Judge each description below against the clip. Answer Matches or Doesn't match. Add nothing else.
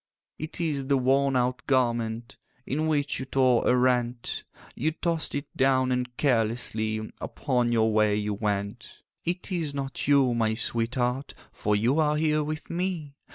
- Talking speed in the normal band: Matches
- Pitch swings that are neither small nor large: Matches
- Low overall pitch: Matches